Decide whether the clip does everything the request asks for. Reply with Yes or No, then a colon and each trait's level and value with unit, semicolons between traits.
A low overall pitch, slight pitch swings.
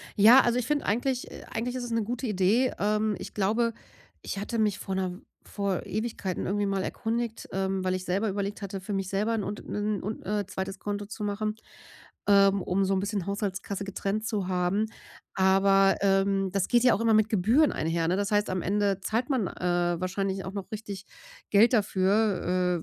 No: high, 200 Hz; narrow, 2.2 semitones